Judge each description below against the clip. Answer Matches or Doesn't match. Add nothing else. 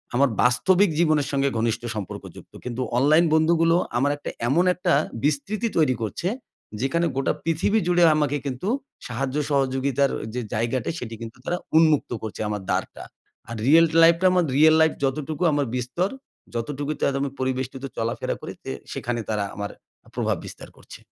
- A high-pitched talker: Doesn't match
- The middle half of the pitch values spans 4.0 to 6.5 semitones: Matches